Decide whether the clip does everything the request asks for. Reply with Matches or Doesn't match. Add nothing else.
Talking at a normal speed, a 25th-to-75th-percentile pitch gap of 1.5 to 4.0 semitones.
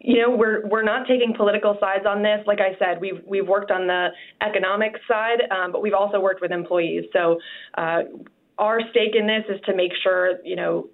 Doesn't match